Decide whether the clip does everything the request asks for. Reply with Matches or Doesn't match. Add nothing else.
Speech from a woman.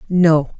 Matches